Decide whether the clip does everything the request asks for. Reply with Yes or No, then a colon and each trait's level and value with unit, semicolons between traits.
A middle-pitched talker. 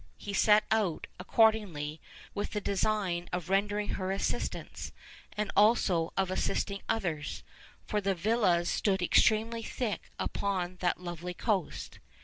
No: high, 195 Hz